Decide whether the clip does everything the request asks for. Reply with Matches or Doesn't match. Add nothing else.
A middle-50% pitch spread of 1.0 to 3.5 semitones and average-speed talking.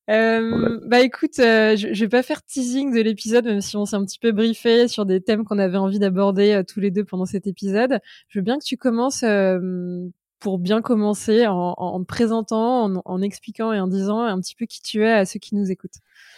Doesn't match